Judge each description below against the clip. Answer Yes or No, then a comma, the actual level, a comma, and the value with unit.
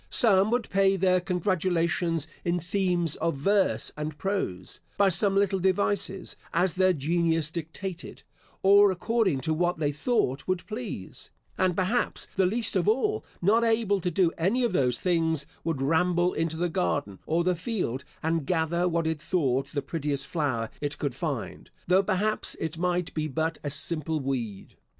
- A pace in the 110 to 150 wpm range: No, average, 165 wpm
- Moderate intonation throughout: Yes, average, 3.8 semitones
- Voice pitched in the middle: Yes, medium, 175 Hz